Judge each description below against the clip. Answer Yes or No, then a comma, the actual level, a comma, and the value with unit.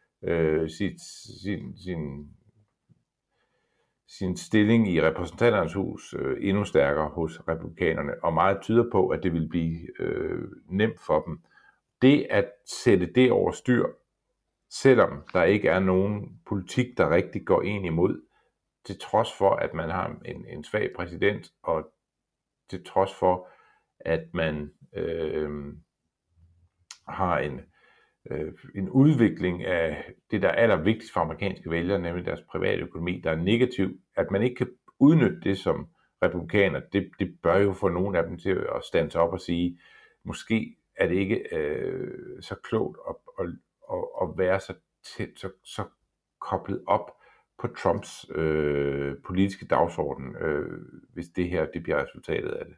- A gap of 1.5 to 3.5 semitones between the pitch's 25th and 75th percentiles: No, average, 4.5 semitones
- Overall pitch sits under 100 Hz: Yes, very low, 90 Hz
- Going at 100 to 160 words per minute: Yes, average, 150 wpm